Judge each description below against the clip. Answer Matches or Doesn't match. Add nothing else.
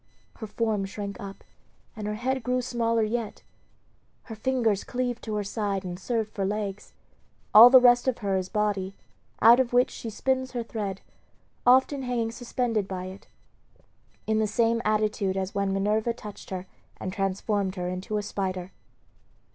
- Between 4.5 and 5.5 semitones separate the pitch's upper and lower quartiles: Doesn't match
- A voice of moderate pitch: Doesn't match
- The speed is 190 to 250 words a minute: Doesn't match